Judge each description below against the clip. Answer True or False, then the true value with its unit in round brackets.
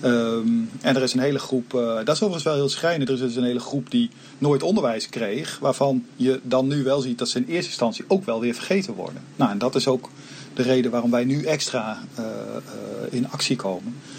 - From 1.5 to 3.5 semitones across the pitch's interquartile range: True (2.4 semitones)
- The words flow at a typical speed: False (235 wpm)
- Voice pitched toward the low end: True (130 Hz)